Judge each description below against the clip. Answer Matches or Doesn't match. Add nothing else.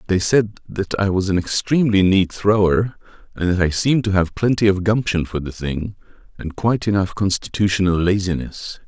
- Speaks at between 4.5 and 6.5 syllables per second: Matches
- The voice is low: Matches